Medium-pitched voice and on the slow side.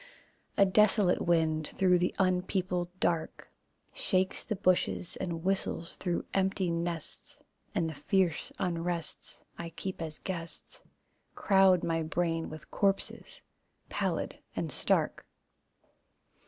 Yes: medium, 175 Hz; slow, 115 wpm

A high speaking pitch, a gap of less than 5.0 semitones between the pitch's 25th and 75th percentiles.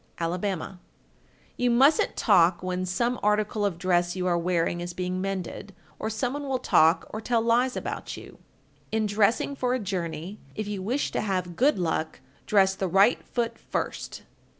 Yes: high, 195 Hz; average, 4.3 semitones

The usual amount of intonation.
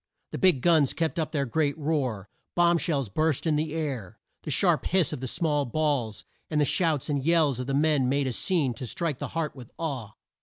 Yes: average, 3.7 semitones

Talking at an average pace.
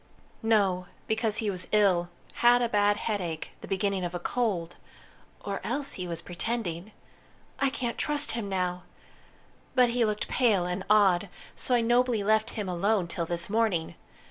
Yes: average, 165 wpm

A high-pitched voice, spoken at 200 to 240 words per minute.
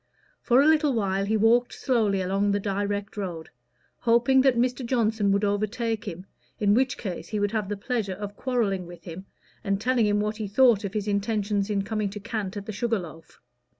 Yes: high, 210 Hz; fast, 205 wpm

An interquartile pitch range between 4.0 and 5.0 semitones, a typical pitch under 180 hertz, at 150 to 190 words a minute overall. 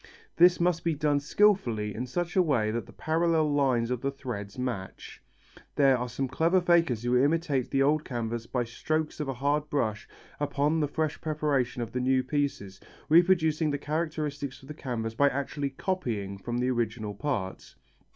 Yes: average, 4.4 semitones; medium, 140 Hz; average, 180 wpm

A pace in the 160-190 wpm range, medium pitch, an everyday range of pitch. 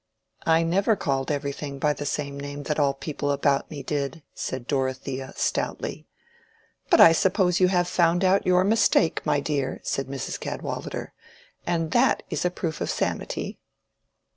Yes: average, 165 wpm; medium, 150 Hz; average, 4.0 semitones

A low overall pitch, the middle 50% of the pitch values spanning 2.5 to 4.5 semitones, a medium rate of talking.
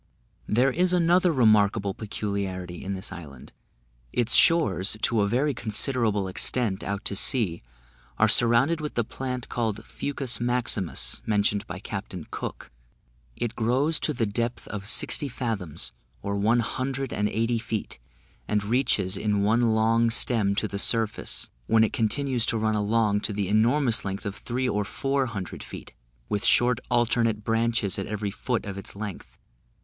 Yes: low, 110 Hz; average, 3.2 semitones; average, 160 wpm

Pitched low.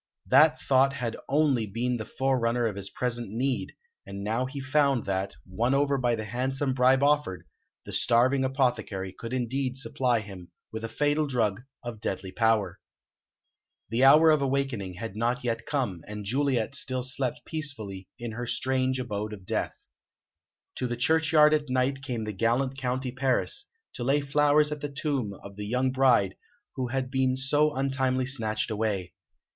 Yes: low, 125 Hz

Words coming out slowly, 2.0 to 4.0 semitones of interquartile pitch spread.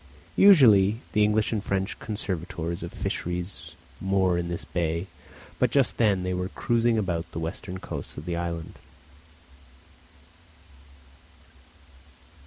Yes: slow, 120 wpm; average, 3.5 semitones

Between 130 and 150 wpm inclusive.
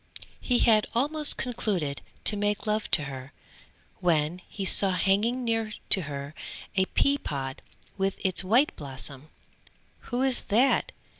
Yes: average, 140 wpm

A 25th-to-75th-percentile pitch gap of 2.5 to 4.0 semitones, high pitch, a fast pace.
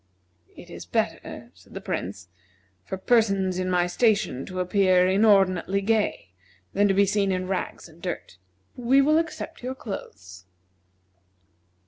No: average, 2.9 semitones; high, 195 Hz; average, 140 wpm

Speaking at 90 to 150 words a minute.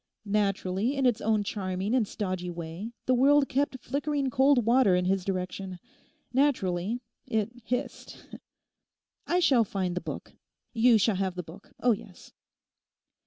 Yes: average, 145 wpm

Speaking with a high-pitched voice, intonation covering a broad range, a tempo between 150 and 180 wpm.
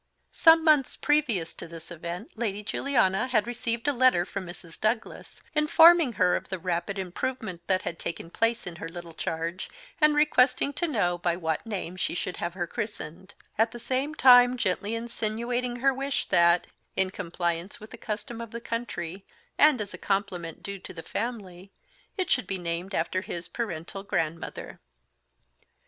Yes: high, 200 Hz; wide, 5.8 semitones; average, 170 wpm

